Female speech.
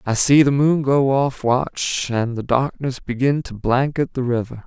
No: male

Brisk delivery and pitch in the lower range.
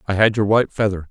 Yes: fast, 270 wpm; low, 105 Hz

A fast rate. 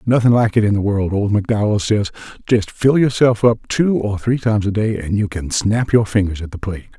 Yes: fast, 240 wpm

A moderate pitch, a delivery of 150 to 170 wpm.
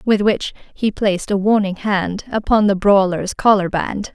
No: high, 200 Hz; average, 160 wpm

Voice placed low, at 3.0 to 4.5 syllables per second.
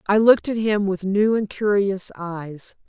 No: high, 200 Hz; 4.2 syllables/s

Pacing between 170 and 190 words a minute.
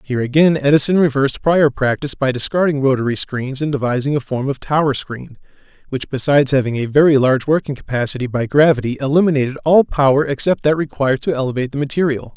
Yes: average, 180 wpm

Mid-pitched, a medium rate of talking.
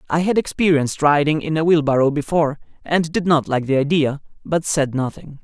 Yes: medium, 150 Hz; average, 190 wpm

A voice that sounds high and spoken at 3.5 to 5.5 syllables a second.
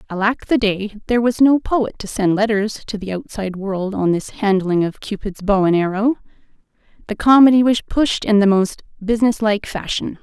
Yes: high, 210 Hz; 5.1 syllables/s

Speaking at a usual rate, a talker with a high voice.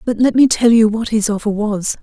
No: fast, 265 wpm; high, 220 Hz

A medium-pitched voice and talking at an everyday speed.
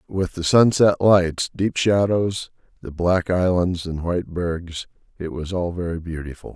No: very low, 90 Hz; average, 155 wpm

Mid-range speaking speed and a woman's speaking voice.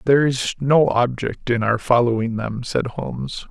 No: average, 170 wpm; male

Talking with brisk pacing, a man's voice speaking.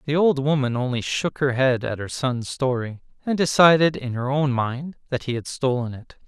Yes: fast, 210 wpm; male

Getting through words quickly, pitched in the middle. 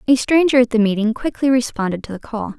No: fast, 230 wpm; high, 240 Hz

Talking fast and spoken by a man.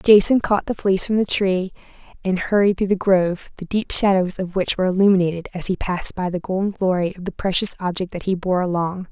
No: fast, 225 wpm; female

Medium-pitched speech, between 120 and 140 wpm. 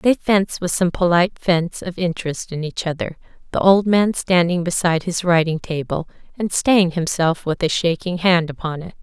No: medium, 175 Hz; average, 185 wpm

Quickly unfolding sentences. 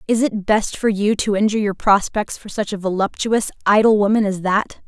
Yes: fast, 210 wpm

